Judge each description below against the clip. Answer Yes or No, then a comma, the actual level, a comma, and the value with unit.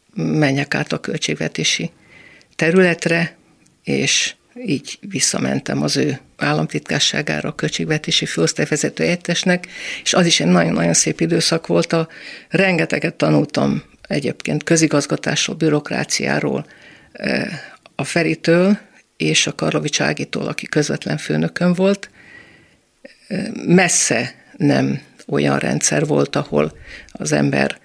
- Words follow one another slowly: Yes, slow, 100 wpm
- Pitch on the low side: No, medium, 160 Hz